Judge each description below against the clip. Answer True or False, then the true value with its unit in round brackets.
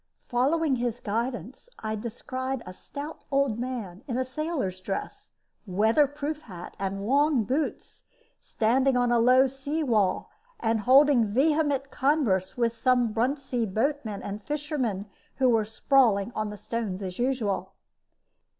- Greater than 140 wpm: False (135 wpm)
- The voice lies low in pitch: False (245 Hz)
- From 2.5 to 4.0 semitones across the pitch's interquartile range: False (4.4 semitones)